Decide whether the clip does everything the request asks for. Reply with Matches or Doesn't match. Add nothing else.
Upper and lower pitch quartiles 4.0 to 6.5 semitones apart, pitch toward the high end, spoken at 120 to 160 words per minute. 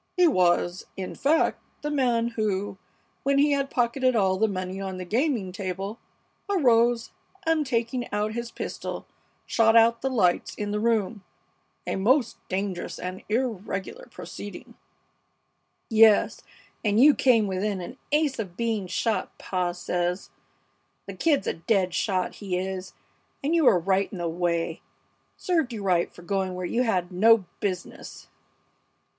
Matches